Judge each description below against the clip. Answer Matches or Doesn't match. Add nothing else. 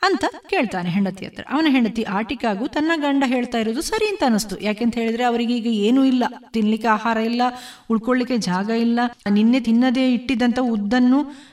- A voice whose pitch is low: Doesn't match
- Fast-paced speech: Matches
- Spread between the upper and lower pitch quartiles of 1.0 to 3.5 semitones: Matches